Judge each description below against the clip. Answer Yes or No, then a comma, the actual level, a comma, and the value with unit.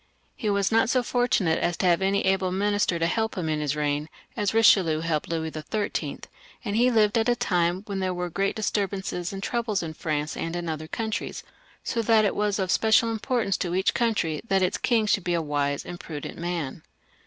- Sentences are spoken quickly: Yes, fast, 210 wpm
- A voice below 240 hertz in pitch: Yes, high, 190 Hz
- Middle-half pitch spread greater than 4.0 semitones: Yes, average, 4.5 semitones